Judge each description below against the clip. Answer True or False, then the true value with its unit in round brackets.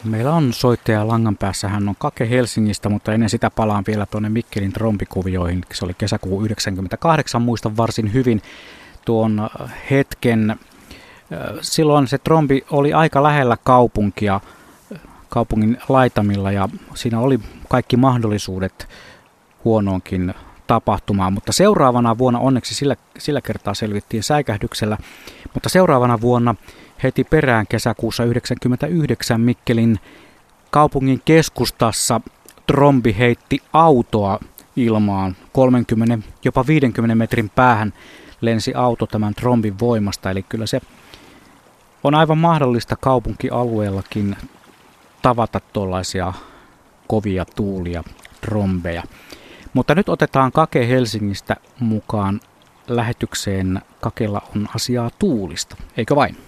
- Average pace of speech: True (105 wpm)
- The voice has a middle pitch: False (115 Hz)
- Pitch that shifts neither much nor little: True (3.6 semitones)